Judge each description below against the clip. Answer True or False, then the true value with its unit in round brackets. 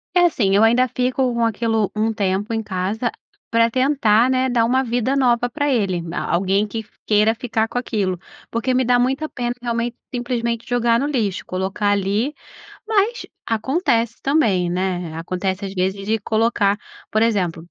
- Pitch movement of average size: True (3.7 semitones)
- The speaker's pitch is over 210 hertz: True (230 Hz)